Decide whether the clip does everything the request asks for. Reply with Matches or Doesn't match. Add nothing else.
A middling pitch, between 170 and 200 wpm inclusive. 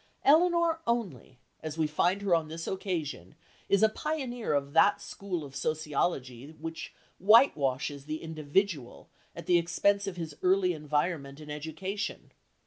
Doesn't match